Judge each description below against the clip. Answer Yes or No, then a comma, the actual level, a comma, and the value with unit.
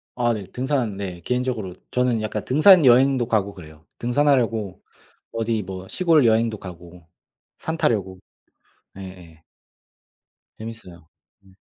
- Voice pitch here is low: Yes, low, 110 Hz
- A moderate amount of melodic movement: Yes, average, 5.0 semitones